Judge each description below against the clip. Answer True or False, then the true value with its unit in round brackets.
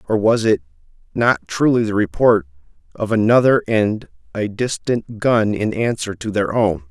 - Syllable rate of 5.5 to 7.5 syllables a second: False (4.5 syllables/s)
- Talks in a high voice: False (105 Hz)